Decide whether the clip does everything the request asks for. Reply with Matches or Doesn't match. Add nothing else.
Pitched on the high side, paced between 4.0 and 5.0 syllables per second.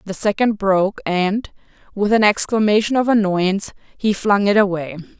Matches